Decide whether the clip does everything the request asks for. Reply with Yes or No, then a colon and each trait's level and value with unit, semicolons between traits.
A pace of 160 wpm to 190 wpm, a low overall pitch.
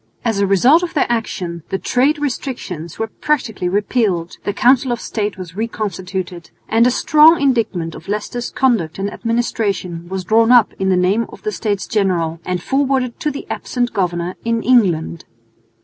No: average, 170 wpm; high, 210 Hz